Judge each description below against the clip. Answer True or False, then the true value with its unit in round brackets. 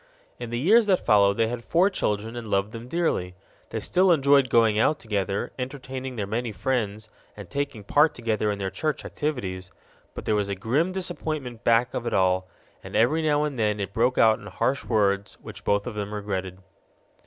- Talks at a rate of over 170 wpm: True (200 wpm)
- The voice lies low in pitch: True (115 Hz)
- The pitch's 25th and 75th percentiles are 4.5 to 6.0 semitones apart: True (5.3 semitones)